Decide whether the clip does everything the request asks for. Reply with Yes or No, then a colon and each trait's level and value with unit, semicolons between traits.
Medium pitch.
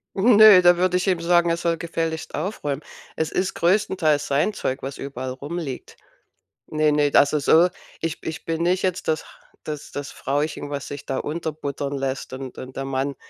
Yes: medium, 155 Hz